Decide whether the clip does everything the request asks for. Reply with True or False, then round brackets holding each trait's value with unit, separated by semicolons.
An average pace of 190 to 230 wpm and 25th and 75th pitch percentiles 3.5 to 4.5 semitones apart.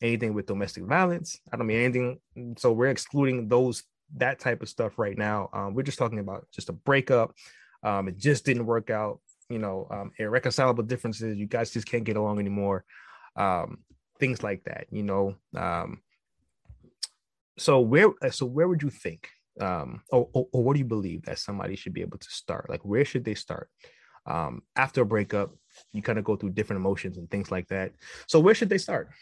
True (200 wpm; 4.0 semitones)